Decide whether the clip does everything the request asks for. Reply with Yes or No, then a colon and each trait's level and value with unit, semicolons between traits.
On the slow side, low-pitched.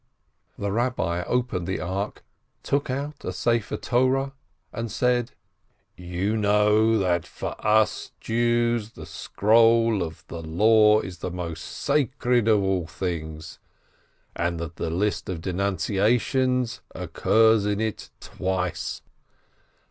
Yes: slow, 130 wpm; low, 105 Hz